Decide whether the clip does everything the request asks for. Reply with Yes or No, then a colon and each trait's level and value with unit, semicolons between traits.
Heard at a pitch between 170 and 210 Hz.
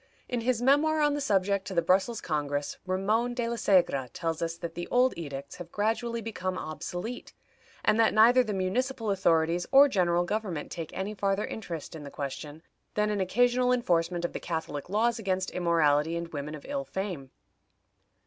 Yes: high, 190 Hz